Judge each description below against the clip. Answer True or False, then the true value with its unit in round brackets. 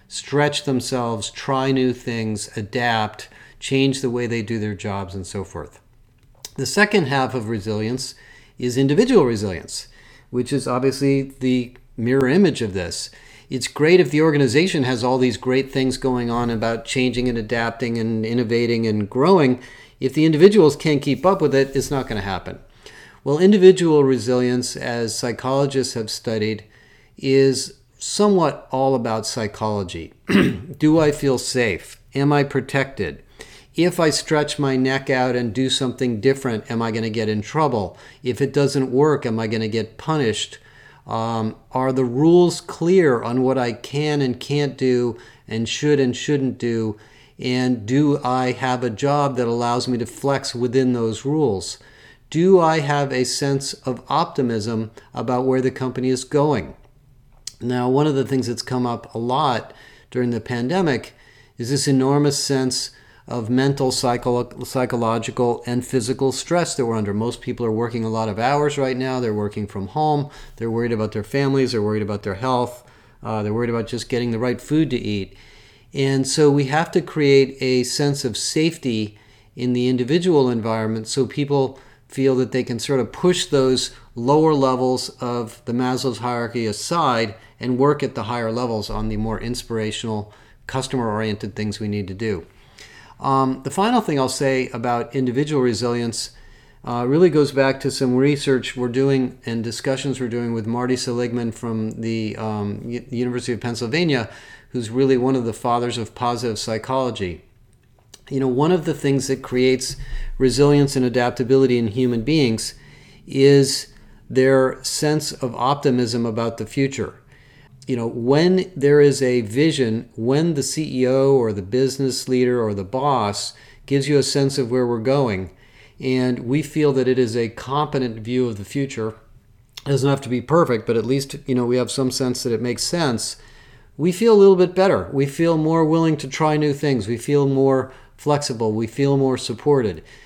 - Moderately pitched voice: False (130 Hz)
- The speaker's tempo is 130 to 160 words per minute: False (175 wpm)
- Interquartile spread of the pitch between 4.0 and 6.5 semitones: False (2.9 semitones)